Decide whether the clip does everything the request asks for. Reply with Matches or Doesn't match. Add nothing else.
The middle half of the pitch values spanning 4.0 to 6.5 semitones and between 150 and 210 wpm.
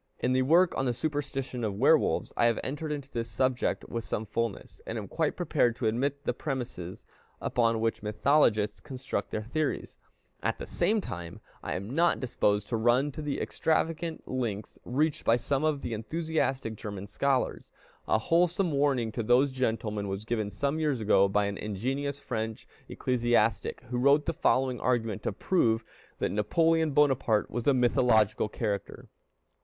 Matches